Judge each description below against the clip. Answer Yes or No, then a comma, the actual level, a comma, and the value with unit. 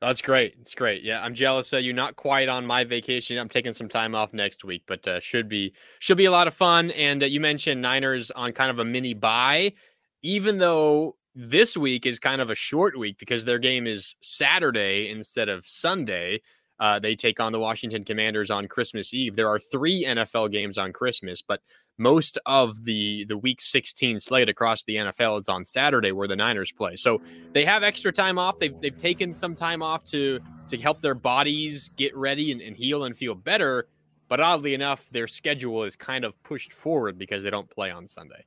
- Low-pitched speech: Yes, low, 125 Hz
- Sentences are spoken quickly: Yes, fast, 210 wpm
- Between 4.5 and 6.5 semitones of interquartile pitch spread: Yes, average, 5.1 semitones